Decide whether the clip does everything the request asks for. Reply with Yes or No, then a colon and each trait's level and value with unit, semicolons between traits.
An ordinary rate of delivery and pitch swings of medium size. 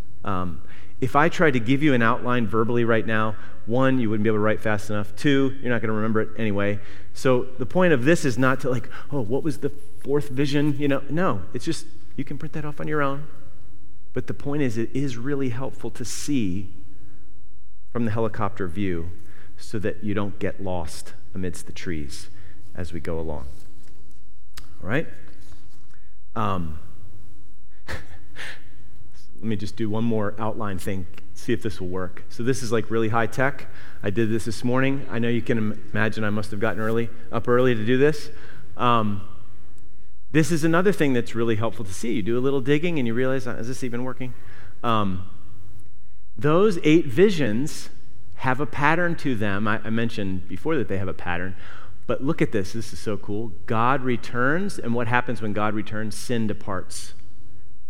Yes: average, 190 wpm; average, 4.4 semitones